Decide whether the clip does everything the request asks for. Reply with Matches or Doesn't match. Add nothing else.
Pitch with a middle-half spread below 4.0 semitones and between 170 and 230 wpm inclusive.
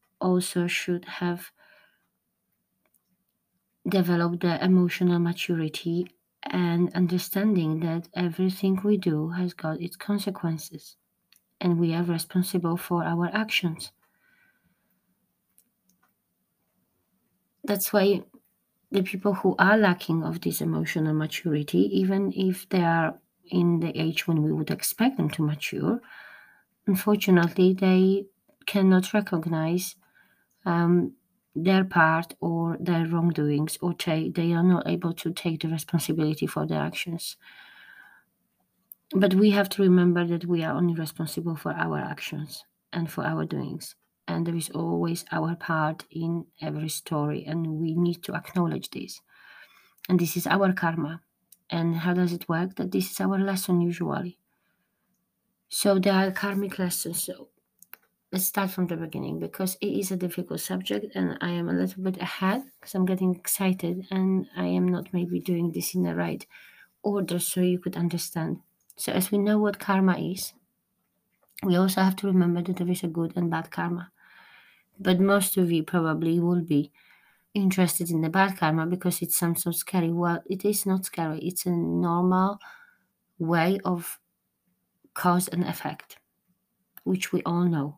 Doesn't match